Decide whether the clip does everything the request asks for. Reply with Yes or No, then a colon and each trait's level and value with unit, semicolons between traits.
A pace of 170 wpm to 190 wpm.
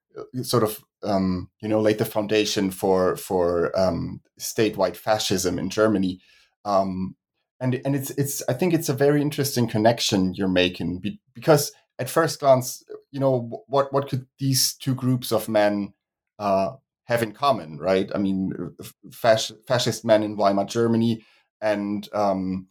No: average, 155 wpm